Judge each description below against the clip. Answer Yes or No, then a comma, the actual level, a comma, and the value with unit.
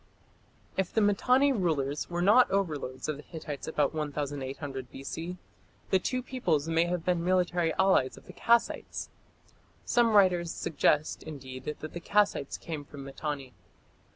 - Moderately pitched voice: Yes, medium, 165 Hz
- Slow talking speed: No, average, 145 wpm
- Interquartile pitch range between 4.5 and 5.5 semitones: Yes, average, 4.8 semitones